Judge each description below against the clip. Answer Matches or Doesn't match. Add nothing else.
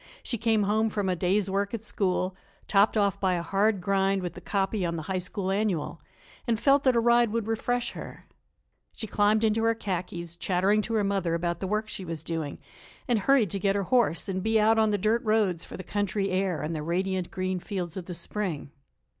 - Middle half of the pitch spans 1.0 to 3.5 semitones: Matches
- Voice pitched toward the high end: Matches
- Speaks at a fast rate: Matches